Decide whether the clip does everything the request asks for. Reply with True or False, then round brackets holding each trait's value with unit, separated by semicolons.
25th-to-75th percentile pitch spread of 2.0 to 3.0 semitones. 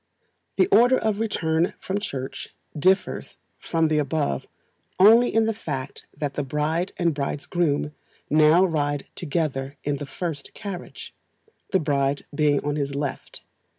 False (4.2 semitones)